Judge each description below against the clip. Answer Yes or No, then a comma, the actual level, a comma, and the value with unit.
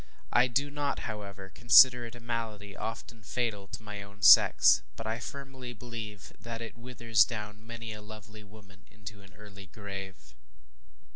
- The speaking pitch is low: Yes, low, 110 Hz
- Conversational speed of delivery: Yes, average, 160 wpm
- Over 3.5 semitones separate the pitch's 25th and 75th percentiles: No, narrow, 2.6 semitones